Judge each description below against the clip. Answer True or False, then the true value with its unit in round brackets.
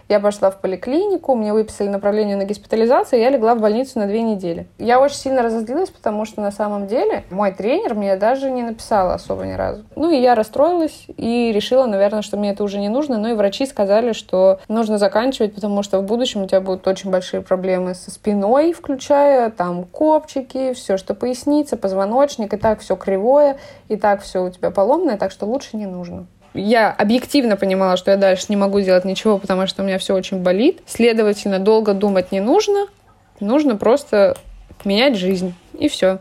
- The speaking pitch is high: True (215 Hz)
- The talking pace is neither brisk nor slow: False (195 wpm)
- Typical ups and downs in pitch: True (4.9 semitones)